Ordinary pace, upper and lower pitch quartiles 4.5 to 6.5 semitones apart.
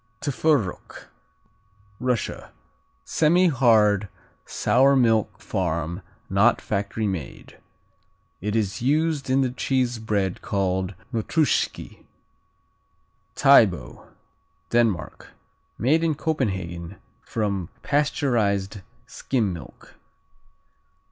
No: slow, 75 wpm; wide, 5.5 semitones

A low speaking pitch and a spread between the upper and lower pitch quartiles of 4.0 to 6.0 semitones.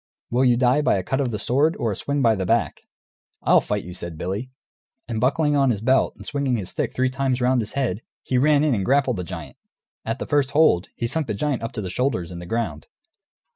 Yes: low, 125 Hz; average, 4.8 semitones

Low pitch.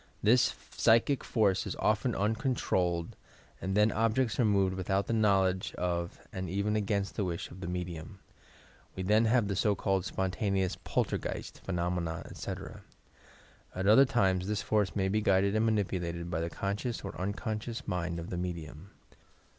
Yes: low, 100 Hz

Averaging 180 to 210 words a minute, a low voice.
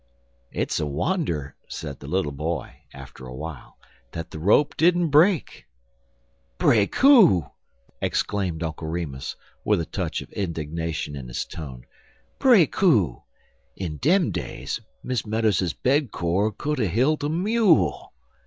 No: slow, 135 wpm; very low, 95 Hz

